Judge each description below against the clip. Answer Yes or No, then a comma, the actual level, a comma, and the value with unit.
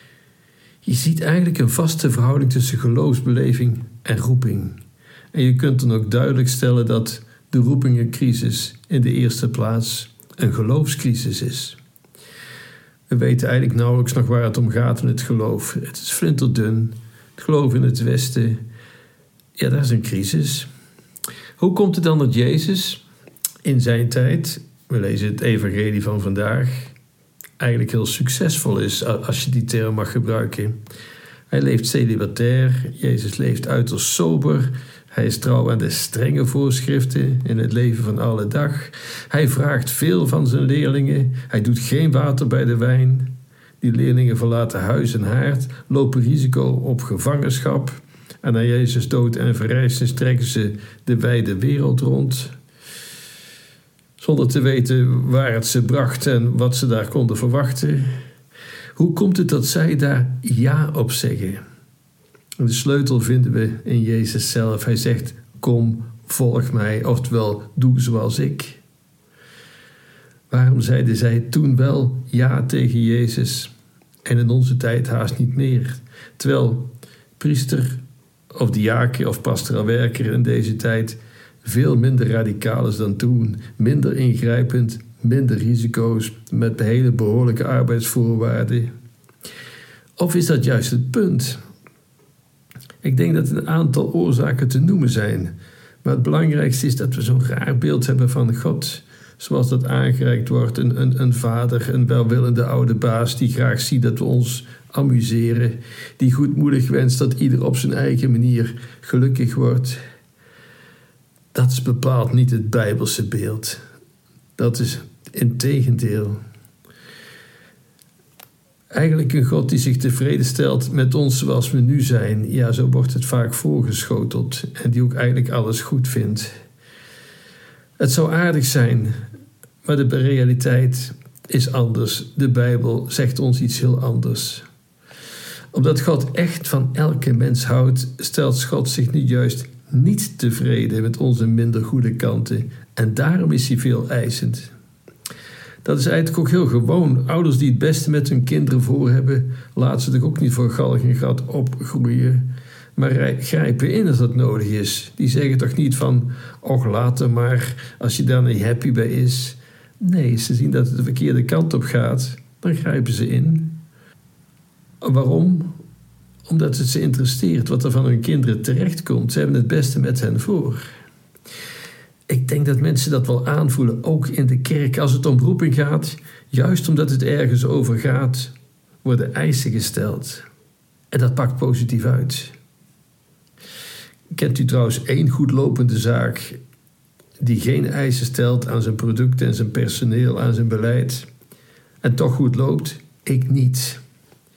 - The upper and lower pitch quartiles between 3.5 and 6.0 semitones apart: No, narrow, 2.4 semitones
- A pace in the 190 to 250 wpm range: No, average, 150 wpm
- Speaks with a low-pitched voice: Yes, low, 125 Hz